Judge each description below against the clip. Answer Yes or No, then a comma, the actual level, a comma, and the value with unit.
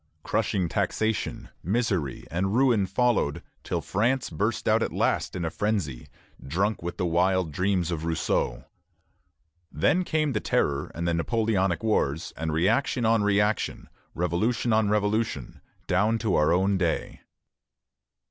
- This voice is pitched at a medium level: No, very low, 95 Hz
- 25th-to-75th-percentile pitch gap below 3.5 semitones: No, average, 4.7 semitones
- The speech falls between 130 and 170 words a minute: Yes, average, 140 wpm